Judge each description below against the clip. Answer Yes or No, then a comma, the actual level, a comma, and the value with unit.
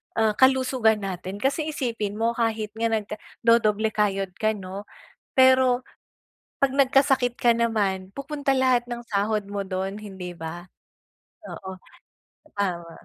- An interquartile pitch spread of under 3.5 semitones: No, average, 4.2 semitones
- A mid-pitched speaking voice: No, high, 220 Hz